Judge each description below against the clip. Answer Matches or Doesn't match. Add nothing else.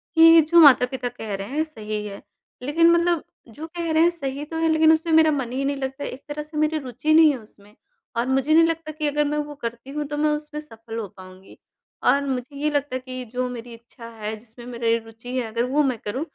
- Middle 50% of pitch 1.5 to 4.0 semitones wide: Doesn't match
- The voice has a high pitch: Matches